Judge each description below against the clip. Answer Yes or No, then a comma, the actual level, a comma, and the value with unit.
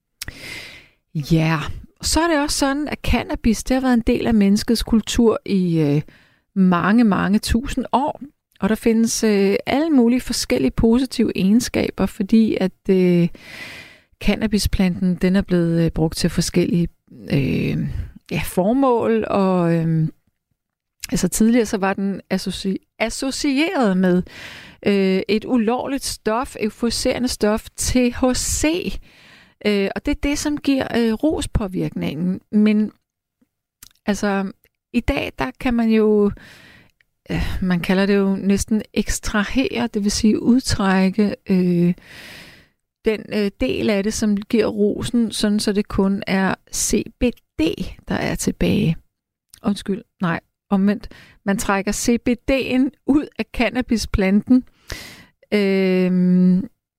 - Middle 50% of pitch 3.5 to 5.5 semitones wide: Yes, average, 3.9 semitones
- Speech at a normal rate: No, slow, 125 wpm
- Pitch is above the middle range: Yes, high, 210 Hz